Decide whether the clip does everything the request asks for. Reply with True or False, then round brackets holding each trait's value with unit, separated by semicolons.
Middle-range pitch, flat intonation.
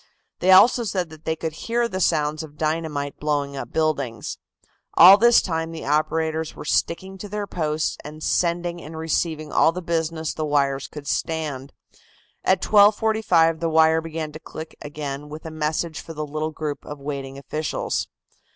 True (160 Hz; 2.1 semitones)